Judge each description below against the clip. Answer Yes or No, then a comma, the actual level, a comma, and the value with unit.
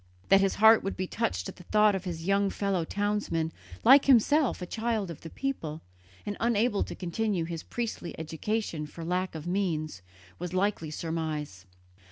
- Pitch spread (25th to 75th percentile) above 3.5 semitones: Yes, average, 4.4 semitones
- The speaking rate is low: No, average, 180 wpm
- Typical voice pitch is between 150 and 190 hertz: Yes, medium, 185 Hz